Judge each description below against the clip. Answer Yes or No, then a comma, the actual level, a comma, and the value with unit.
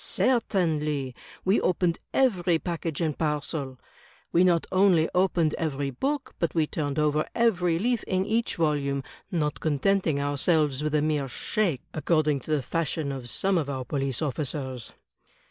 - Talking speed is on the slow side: No, average, 150 wpm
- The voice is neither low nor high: Yes, medium, 155 Hz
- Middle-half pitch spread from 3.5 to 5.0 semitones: Yes, average, 3.9 semitones